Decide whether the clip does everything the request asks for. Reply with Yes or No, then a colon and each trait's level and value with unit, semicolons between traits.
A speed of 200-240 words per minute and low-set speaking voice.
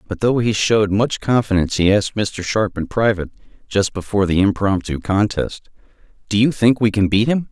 No: average, 190 wpm; low, 105 Hz